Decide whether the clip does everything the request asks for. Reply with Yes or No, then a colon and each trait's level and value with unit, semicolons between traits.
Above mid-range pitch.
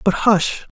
Yes: high, 200 Hz